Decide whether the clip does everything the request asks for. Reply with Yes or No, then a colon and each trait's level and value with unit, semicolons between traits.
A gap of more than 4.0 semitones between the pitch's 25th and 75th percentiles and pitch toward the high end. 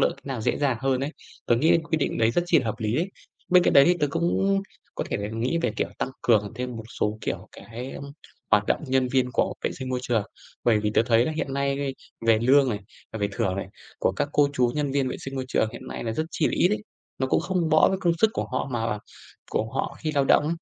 No: average, 4.9 semitones; low, 130 Hz